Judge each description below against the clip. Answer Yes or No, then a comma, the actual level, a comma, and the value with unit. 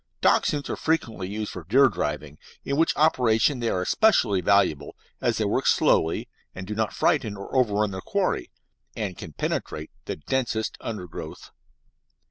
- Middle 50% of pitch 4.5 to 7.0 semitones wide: Yes, wide, 5.5 semitones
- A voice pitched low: Yes, low, 105 Hz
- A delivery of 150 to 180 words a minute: Yes, average, 155 wpm